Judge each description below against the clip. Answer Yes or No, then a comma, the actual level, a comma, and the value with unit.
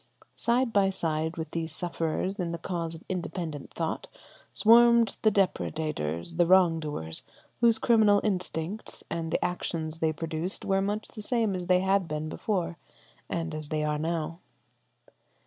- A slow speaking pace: No, average, 155 wpm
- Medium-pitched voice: Yes, medium, 170 Hz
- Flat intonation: No, average, 3.8 semitones